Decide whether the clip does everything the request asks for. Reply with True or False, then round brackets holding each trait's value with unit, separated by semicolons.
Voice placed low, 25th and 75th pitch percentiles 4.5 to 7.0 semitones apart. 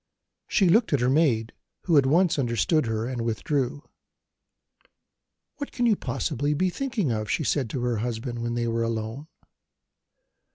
True (130 Hz; 5.5 semitones)